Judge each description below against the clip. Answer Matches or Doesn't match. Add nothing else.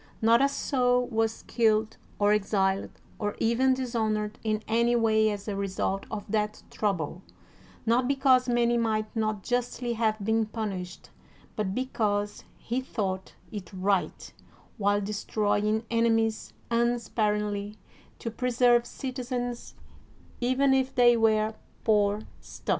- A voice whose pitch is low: Doesn't match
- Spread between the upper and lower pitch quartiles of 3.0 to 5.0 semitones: Doesn't match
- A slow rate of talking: Matches